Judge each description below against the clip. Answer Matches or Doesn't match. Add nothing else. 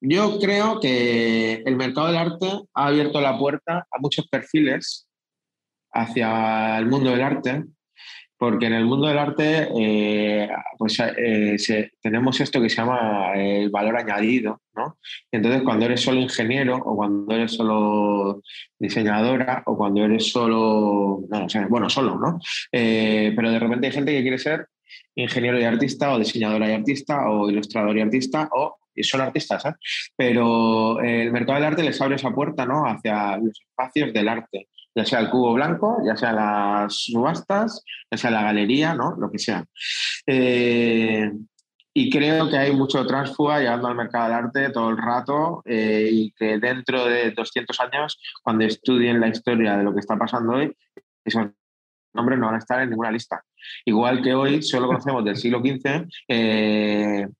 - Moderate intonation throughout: Matches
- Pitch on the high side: Doesn't match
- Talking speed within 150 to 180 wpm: Matches